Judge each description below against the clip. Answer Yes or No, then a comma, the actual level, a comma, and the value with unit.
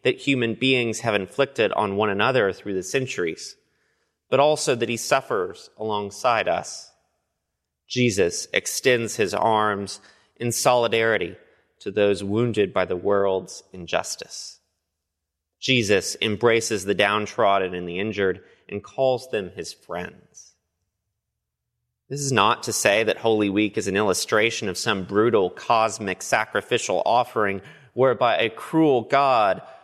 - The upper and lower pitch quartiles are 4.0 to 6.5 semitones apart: Yes, average, 4.3 semitones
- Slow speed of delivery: Yes, slow, 130 wpm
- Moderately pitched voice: No, low, 105 Hz